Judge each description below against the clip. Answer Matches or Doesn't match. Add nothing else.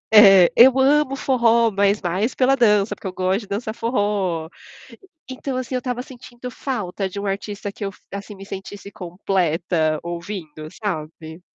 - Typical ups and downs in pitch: Matches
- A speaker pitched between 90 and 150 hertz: Doesn't match